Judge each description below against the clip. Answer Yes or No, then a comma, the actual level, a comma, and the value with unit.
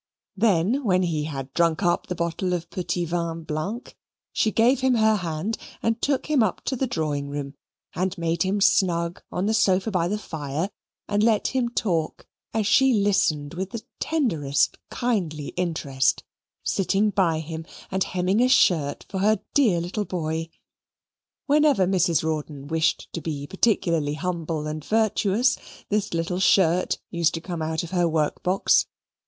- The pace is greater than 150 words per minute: Yes, average, 165 wpm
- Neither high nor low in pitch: Yes, medium, 180 Hz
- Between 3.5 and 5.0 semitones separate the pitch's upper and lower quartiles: Yes, average, 4.5 semitones